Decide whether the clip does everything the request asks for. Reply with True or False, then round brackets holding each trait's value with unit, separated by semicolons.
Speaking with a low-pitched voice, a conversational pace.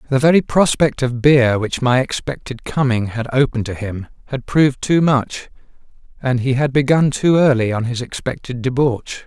True (130 Hz; 175 wpm)